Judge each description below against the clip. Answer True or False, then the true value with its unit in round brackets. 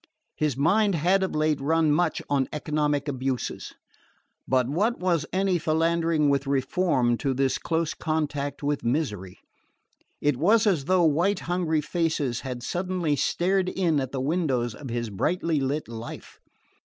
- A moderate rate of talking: True (150 wpm)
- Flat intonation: False (4.2 semitones)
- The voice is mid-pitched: True (150 Hz)